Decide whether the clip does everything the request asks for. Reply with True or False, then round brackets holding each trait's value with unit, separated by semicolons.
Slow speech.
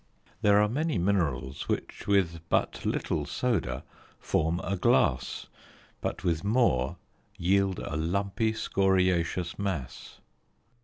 True (110 wpm)